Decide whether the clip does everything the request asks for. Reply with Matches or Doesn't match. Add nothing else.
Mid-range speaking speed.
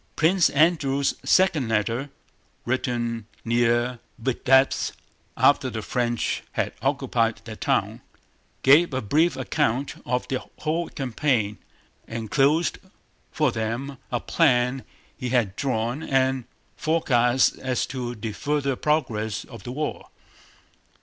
Doesn't match